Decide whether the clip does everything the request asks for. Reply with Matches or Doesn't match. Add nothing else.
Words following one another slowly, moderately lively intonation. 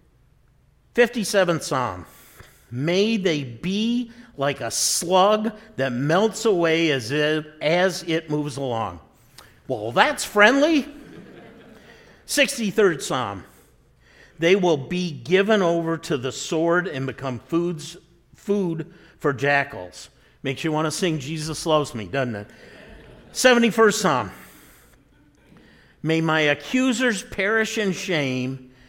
Doesn't match